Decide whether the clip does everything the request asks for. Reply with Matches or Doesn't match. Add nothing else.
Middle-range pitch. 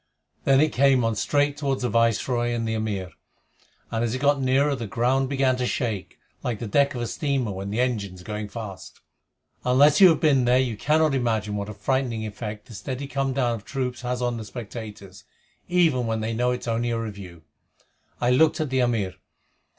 Doesn't match